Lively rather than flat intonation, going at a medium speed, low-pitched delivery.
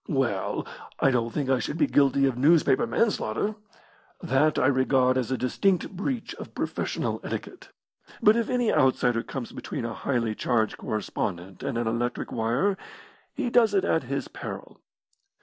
Yes: wide, 6.6 semitones; average, 165 wpm; low, 130 Hz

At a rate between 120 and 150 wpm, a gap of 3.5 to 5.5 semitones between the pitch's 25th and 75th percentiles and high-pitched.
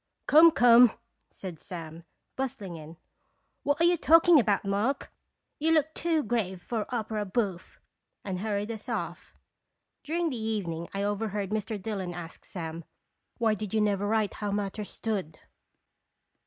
Yes: average, 145 wpm; average, 4.2 semitones; high, 210 Hz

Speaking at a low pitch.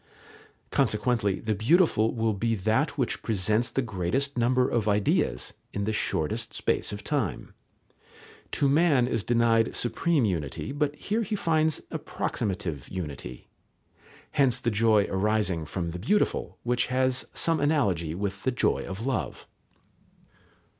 Yes: low, 115 Hz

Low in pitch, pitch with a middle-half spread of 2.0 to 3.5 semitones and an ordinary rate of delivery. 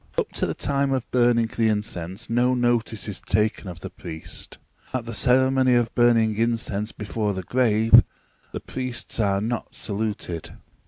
Yes: low, 115 Hz; average, 2.7 semitones; average, 160 wpm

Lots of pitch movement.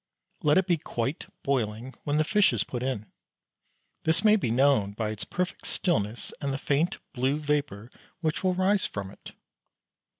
Yes: wide, 6.2 semitones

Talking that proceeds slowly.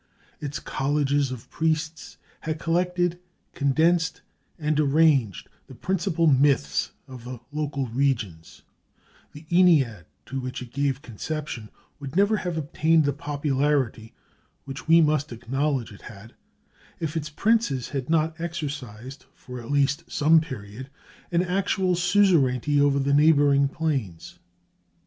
Yes: slow, 125 wpm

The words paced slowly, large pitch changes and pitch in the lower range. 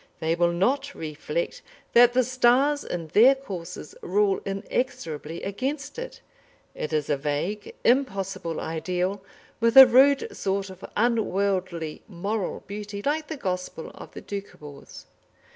No: slow, 130 wpm; wide, 6.7 semitones; high, 200 Hz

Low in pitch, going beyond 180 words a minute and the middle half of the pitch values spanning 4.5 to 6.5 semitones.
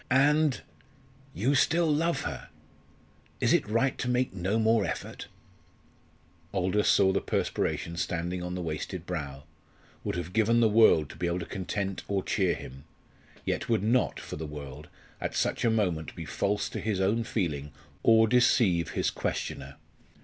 No: very low, 95 Hz; average, 165 wpm; average, 5.2 semitones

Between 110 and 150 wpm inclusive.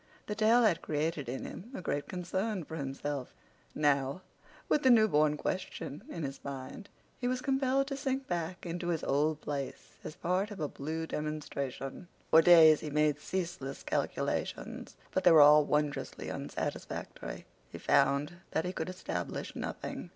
No: average, 160 wpm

